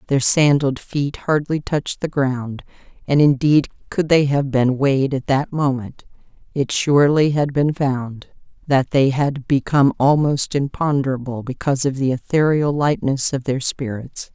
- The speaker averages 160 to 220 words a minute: No, average, 150 wpm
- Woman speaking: Yes, female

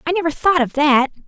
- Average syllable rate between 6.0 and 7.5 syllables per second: Yes, 6.1 syllables/s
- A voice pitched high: Yes, very high, 305 Hz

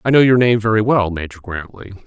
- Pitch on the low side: Yes, low, 105 Hz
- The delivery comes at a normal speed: No, fast, 230 wpm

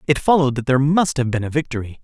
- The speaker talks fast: Yes, fast, 265 wpm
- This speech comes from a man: Yes, male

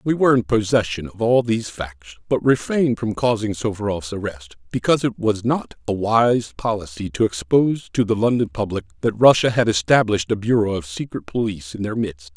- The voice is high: No, low, 105 Hz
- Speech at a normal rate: Yes, average, 190 wpm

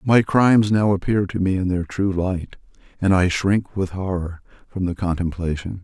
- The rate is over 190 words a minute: No, average, 185 wpm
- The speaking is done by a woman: No, male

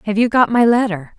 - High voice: Yes, high, 220 Hz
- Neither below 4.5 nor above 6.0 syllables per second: Yes, 5.7 syllables/s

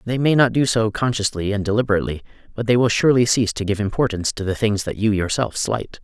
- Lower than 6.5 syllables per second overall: No, 6.6 syllables/s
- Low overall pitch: Yes, low, 110 Hz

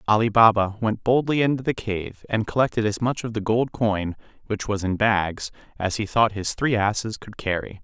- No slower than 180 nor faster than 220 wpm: Yes, fast, 205 wpm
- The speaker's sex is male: Yes, male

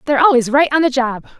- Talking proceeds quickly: Yes, fast, 260 wpm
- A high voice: Yes, very high, 270 Hz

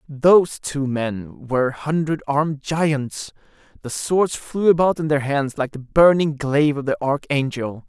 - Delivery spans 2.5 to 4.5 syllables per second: Yes, 4.4 syllables/s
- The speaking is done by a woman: No, male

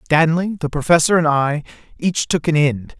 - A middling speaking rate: Yes, average, 180 wpm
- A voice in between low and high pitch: Yes, medium, 155 Hz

